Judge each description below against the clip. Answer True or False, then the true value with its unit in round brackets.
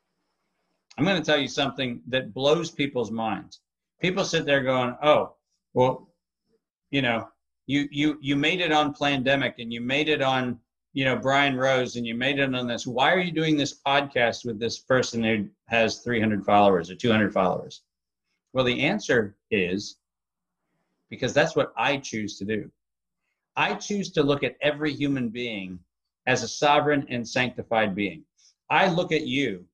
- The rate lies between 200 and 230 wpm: False (170 wpm)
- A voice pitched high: False (130 Hz)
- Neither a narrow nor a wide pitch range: True (4.1 semitones)